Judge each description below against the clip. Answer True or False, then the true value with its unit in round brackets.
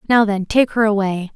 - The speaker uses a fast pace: True (220 wpm)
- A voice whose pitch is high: True (210 Hz)